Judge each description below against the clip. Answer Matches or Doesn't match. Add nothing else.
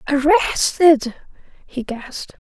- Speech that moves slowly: Matches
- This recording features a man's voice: Doesn't match